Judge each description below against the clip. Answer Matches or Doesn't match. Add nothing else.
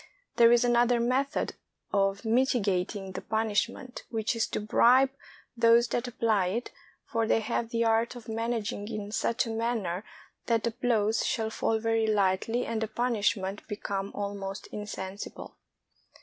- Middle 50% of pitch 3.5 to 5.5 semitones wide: Doesn't match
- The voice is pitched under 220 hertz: Doesn't match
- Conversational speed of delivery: Matches